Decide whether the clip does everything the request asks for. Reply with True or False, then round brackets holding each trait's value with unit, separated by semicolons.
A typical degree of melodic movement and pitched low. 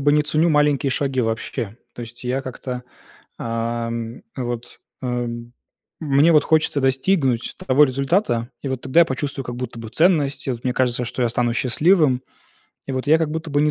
True (3.6 semitones; 130 Hz)